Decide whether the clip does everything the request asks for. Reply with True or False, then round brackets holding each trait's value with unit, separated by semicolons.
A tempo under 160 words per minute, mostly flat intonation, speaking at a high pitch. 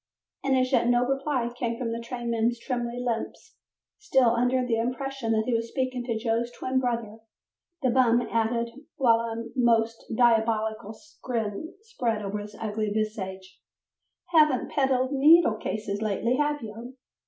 True (145 wpm; 2.3 semitones; 235 Hz)